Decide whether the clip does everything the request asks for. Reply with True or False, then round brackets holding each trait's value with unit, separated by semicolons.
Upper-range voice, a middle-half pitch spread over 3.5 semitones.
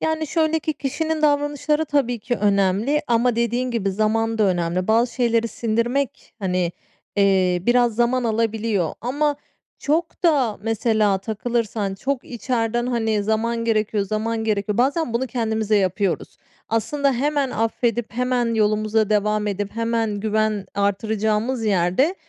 False (225 Hz; 3.0 semitones)